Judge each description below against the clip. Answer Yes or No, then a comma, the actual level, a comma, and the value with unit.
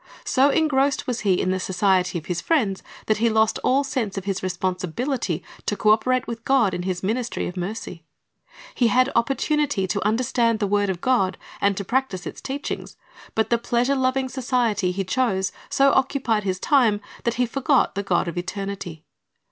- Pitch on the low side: No, high, 220 Hz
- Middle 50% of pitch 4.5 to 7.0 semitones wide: Yes, average, 5.3 semitones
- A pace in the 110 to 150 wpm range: No, average, 185 wpm